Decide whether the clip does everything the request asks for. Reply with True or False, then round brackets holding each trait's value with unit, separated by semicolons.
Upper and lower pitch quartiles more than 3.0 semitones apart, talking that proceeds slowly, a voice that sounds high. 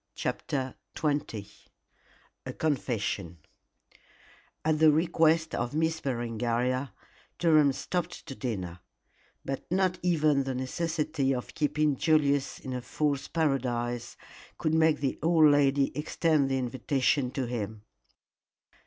False (4.0 semitones; 115 wpm; 140 Hz)